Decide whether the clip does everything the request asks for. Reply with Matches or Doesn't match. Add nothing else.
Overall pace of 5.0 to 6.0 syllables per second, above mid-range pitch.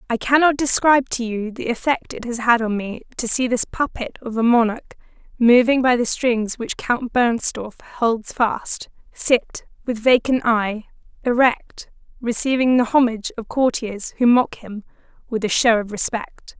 Doesn't match